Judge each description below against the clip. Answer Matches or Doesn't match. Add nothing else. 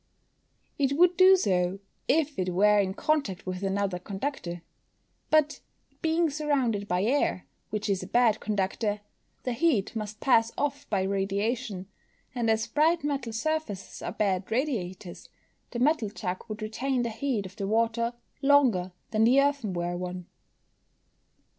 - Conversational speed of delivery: Matches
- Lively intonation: Matches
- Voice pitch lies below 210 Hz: Doesn't match